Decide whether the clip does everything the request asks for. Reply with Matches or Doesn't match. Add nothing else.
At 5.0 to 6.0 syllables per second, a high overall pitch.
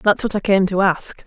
Matches